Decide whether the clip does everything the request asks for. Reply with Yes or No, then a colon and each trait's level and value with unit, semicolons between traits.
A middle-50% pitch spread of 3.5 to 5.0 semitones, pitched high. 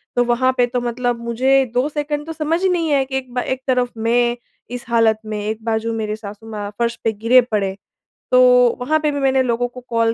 No: narrow, 2.6 semitones; high, 245 Hz